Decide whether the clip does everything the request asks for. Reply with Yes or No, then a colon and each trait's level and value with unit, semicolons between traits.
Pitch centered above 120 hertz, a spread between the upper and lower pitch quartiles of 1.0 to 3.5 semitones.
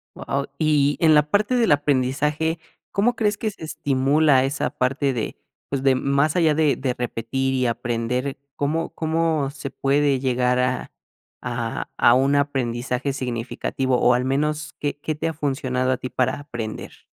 Yes: medium, 140 Hz; average, 2.9 semitones